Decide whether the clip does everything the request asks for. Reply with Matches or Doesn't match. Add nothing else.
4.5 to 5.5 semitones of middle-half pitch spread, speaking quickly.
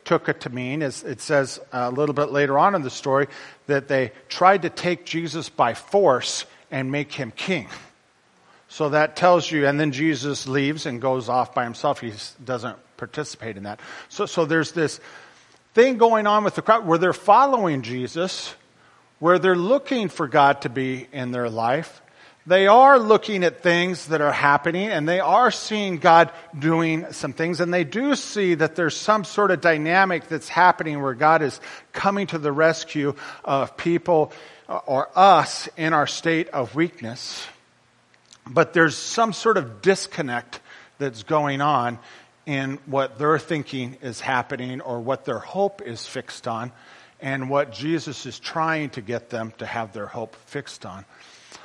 Doesn't match